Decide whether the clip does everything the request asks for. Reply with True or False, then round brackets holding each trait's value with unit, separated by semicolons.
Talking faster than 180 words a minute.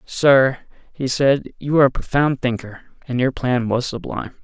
False (175 wpm)